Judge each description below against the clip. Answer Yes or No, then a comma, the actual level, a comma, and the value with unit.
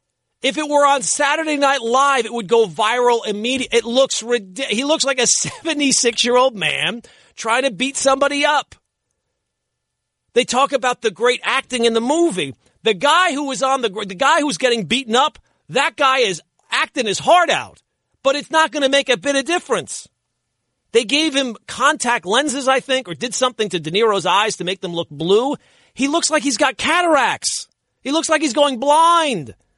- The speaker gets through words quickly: No, average, 190 wpm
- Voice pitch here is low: No, very high, 265 Hz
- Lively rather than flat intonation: No, average, 3.8 semitones